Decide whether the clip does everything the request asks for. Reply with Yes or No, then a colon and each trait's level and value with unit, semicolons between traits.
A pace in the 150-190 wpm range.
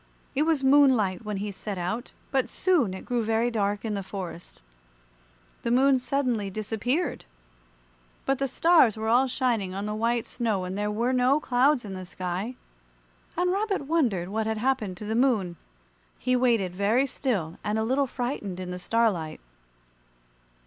Yes: average, 170 wpm